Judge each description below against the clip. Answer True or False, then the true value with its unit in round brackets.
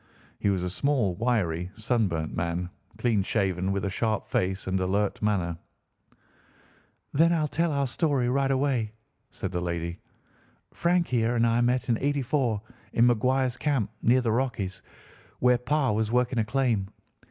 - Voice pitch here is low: True (115 Hz)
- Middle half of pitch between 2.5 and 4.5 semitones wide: False (5.3 semitones)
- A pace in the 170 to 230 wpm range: False (155 wpm)